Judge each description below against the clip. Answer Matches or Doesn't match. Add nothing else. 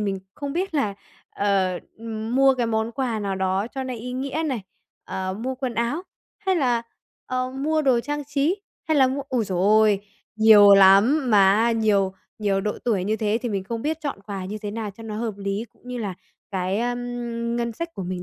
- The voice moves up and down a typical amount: Matches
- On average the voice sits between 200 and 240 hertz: Matches